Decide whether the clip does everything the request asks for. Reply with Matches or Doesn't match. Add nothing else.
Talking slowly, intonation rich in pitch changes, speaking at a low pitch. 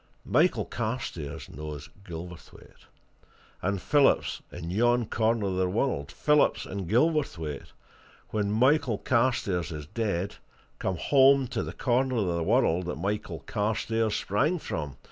Matches